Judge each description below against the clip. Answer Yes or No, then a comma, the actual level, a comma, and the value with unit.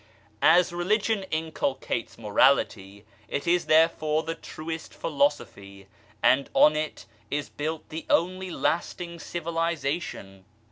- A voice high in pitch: No, medium, 155 Hz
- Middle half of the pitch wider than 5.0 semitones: No, average, 3.6 semitones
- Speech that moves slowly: Yes, slow, 105 wpm